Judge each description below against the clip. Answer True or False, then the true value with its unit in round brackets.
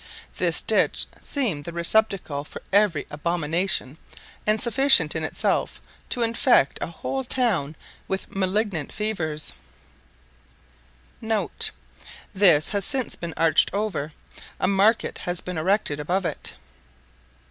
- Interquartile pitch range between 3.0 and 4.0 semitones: False (5.4 semitones)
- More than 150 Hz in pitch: True (190 Hz)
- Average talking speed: False (115 wpm)